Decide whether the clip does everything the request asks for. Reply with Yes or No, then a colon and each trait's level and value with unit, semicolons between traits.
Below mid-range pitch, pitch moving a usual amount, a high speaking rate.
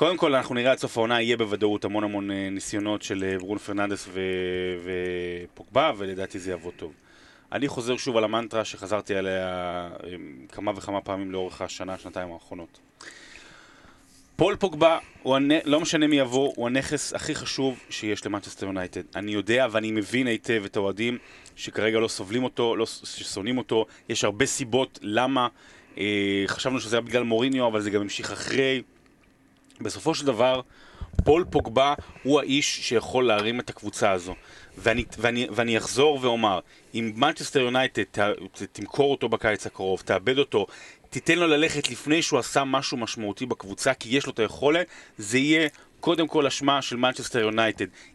Yes: low, 115 Hz; average, 4.7 semitones; fast, 155 wpm